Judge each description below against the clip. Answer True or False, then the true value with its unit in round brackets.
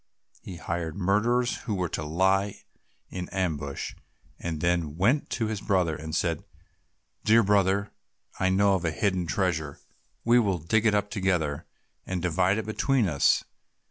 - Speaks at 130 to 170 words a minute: True (160 wpm)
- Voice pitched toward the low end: True (95 Hz)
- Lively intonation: False (3.6 semitones)